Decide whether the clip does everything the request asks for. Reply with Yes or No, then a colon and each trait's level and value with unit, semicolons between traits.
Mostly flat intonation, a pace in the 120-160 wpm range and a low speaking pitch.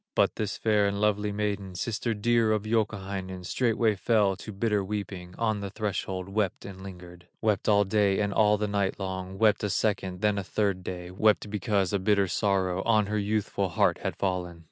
No: narrow, 1.9 semitones; average, 190 wpm; low, 100 Hz